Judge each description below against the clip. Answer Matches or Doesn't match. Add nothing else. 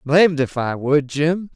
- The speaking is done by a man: Matches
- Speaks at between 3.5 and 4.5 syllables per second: Matches